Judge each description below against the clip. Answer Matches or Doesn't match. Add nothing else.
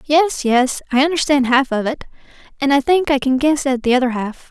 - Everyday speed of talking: Doesn't match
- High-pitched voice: Matches